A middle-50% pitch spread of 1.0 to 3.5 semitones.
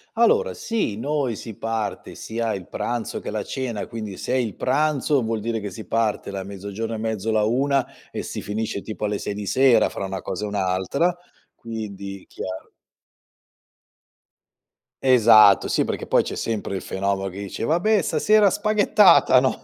No: average, 4.6 semitones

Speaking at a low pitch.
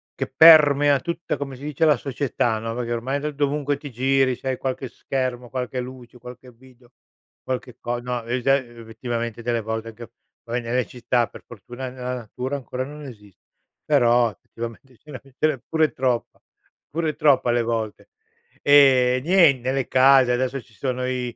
Yes: low, 125 Hz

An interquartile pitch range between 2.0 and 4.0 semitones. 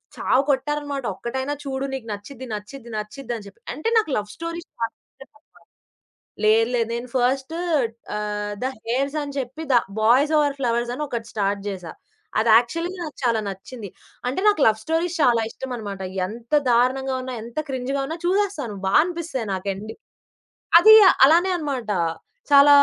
No: average, 4.4 semitones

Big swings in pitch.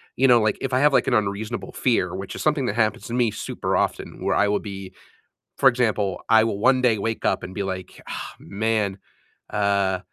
No: average, 3.4 semitones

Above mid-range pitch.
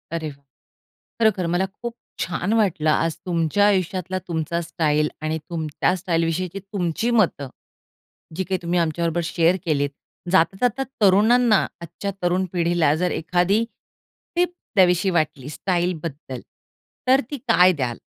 No: medium, 175 Hz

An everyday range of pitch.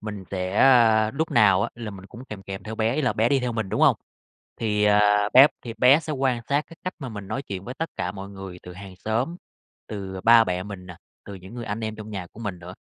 Yes: average, 3.8 semitones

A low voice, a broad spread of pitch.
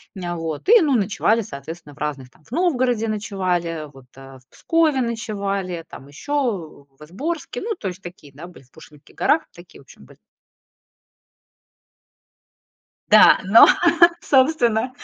No: high, 190 Hz; wide, 8.3 semitones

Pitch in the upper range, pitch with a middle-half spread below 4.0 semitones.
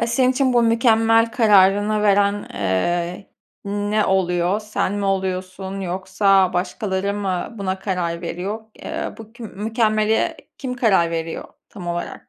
Yes: high, 200 Hz; average, 2.9 semitones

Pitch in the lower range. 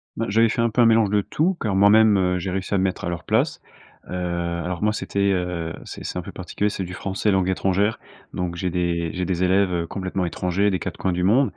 Yes: very low, 95 Hz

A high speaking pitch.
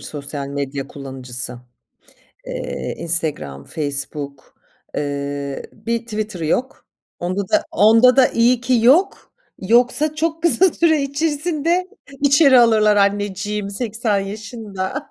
Yes: high, 210 Hz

